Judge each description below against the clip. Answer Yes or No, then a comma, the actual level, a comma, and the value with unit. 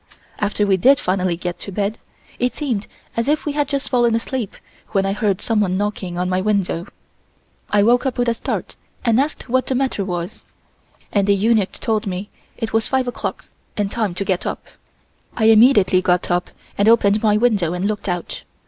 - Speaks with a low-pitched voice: No, high, 210 Hz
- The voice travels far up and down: No, average, 3.9 semitones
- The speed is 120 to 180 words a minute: No, average, 195 wpm